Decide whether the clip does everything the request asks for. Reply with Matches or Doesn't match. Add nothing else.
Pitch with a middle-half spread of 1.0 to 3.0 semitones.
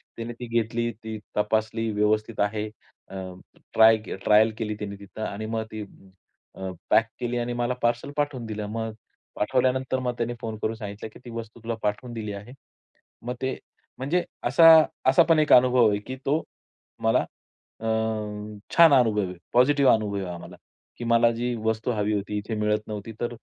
Matches